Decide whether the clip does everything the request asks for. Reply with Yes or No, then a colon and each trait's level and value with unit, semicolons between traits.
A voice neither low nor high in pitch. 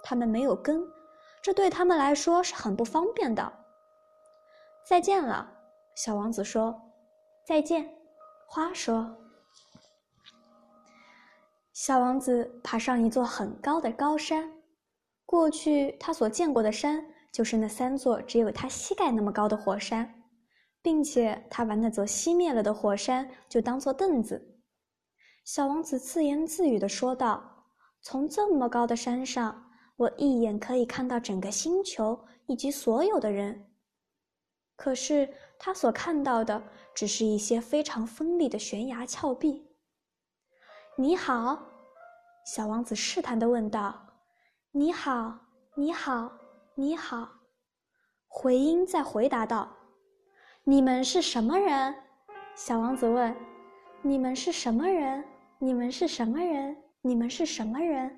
No: very high, 265 Hz